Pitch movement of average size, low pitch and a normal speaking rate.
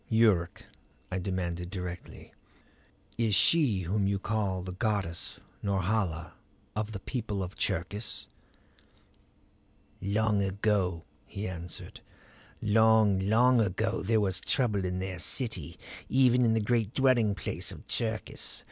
No: average, 3.2 semitones; low, 100 Hz; slow, 120 wpm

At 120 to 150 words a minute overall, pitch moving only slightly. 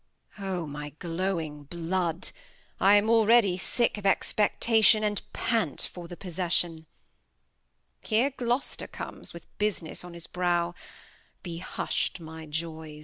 No: slow, 135 wpm; average, 4.0 semitones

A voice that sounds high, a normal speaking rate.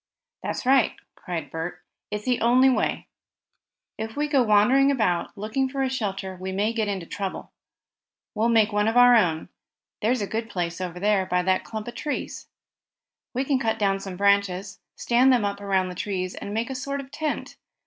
Yes: high, 210 Hz; average, 190 wpm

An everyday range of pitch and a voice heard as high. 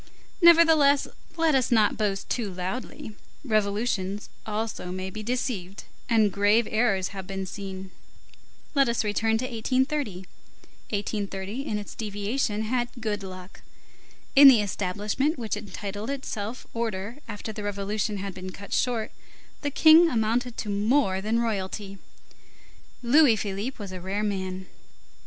Yes: average, 3.5 semitones; high, 210 Hz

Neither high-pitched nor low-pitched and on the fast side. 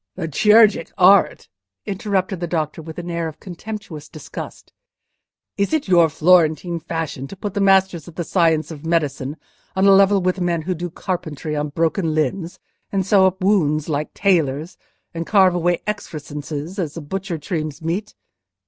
No: medium, 170 Hz; average, 165 wpm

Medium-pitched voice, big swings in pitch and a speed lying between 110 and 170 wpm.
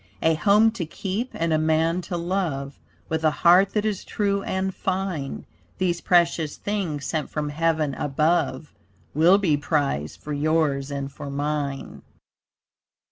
No: medium, 160 Hz; average, 4.1 semitones; average, 145 wpm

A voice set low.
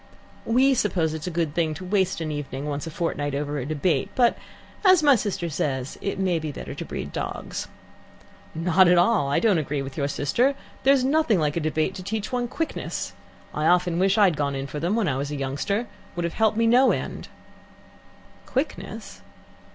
No: medium, 175 Hz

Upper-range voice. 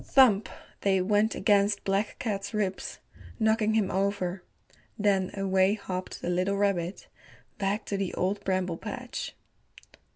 Yes: high, 200 Hz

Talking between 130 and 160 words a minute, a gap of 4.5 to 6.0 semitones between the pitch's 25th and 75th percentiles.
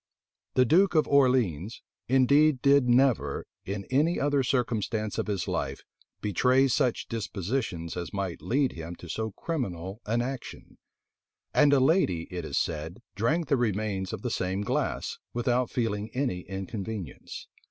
Yes: average, 145 wpm; wide, 5.6 semitones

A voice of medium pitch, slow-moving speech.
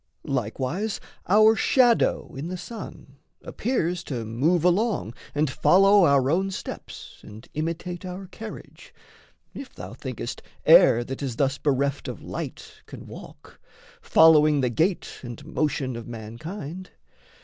Yes: medium, 155 Hz; slow, 130 wpm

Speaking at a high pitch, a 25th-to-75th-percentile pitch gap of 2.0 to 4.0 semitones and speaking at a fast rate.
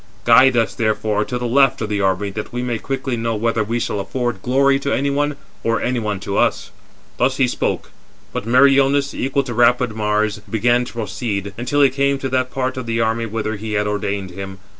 No: low, 120 Hz; average, 3.6 semitones; fast, 215 wpm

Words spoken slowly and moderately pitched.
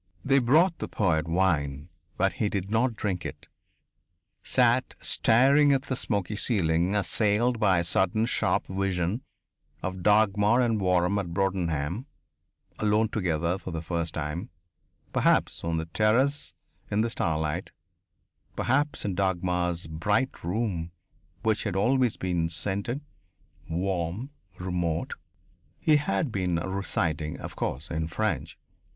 No: slow, 130 wpm; very low, 95 Hz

